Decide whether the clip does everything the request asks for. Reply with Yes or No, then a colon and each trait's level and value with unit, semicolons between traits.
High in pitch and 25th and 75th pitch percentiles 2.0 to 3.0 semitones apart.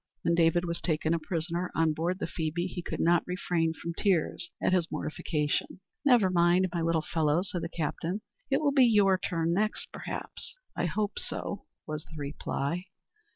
No: medium, 170 Hz; narrow, 2.5 semitones